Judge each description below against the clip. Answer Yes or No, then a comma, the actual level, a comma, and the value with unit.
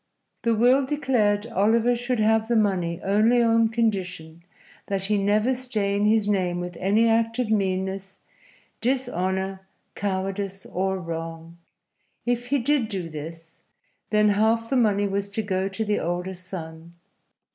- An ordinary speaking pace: Yes, average, 145 wpm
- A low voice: No, high, 205 Hz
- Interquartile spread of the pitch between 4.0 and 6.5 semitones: No, average, 3.4 semitones